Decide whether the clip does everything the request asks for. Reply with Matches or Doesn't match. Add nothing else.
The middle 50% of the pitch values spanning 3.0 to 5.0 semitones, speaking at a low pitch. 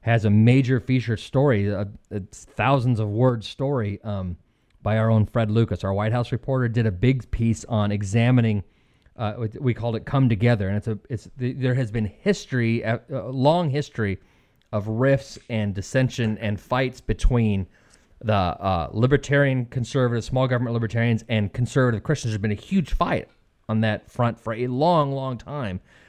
Matches